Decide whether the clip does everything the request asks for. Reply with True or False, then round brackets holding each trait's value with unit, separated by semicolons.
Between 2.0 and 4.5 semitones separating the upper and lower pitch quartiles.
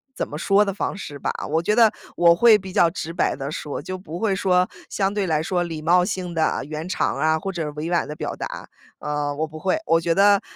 True (3.5 semitones)